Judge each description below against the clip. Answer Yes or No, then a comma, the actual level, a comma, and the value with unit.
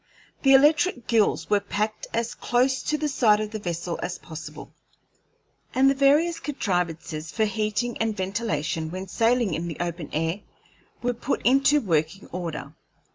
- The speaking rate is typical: Yes, average, 155 wpm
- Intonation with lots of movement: Yes, wide, 6.6 semitones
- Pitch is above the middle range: Yes, high, 215 Hz